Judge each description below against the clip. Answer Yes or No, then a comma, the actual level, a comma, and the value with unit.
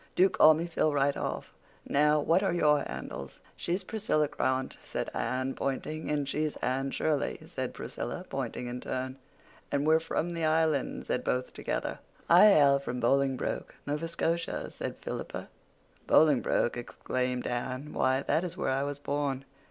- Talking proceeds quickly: No, average, 160 wpm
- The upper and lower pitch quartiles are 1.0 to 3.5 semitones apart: Yes, average, 3.2 semitones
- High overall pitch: No, medium, 145 Hz